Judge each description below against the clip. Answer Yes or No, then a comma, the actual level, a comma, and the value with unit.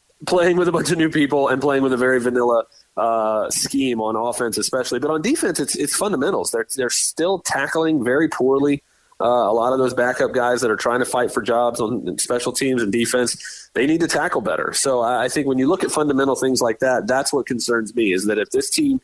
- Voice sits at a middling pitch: No, low, 130 Hz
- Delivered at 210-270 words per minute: Yes, fast, 235 wpm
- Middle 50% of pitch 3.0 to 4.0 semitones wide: Yes, average, 3.7 semitones